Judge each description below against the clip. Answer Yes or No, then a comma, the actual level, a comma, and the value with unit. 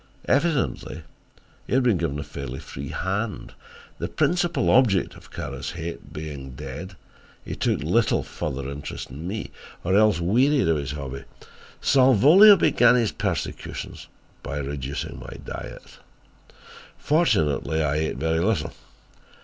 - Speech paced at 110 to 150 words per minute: Yes, slow, 135 wpm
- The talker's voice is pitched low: Yes, very low, 85 Hz